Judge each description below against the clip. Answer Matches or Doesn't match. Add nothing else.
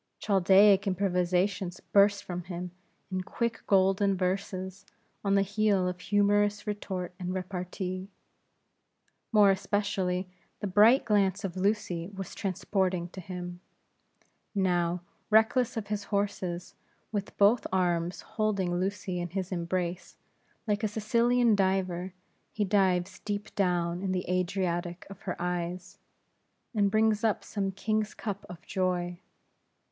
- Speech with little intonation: Matches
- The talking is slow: Matches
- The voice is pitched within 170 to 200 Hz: Matches